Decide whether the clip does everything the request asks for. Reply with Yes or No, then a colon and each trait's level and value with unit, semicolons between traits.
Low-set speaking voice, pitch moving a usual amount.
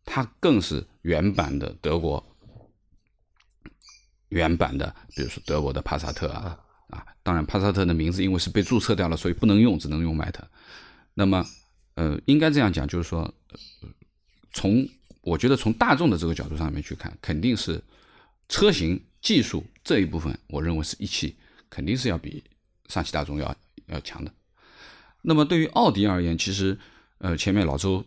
Yes: very low, 90 Hz; average, 4.0 semitones